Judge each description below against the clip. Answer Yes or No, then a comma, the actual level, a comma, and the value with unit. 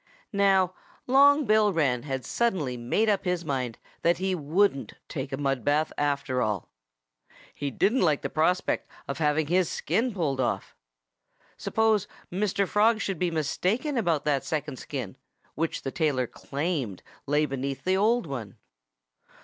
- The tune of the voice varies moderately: No, wide, 6.2 semitones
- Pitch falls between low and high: Yes, medium, 160 Hz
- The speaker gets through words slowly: No, average, 150 wpm